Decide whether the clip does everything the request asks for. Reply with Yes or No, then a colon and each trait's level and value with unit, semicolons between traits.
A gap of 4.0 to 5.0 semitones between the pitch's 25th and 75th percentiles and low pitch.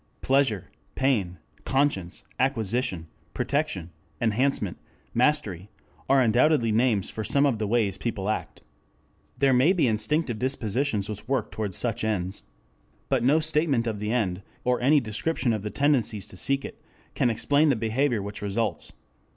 Yes: average, 4.7 semitones; low, 115 Hz